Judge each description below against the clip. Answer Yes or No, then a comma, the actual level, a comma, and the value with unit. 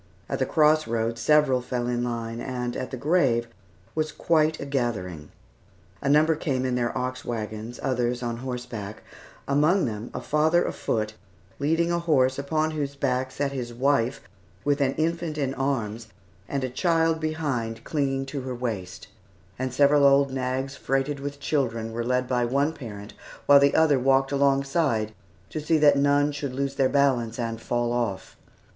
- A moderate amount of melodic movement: Yes, average, 3.2 semitones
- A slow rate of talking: No, average, 170 wpm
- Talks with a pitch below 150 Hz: Yes, low, 135 Hz